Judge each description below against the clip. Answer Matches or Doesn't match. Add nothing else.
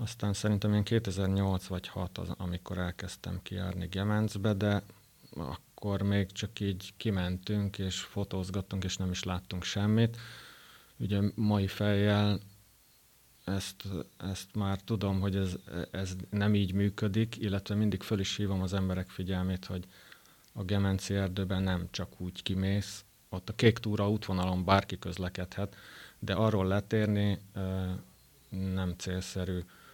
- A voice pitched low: Matches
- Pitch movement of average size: Doesn't match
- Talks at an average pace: Matches